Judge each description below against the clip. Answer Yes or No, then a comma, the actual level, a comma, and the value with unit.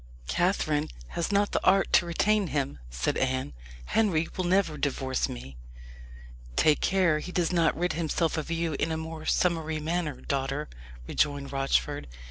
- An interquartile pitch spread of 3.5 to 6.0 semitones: Yes, average, 3.9 semitones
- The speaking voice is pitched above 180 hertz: No, medium, 160 Hz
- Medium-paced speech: Yes, average, 155 wpm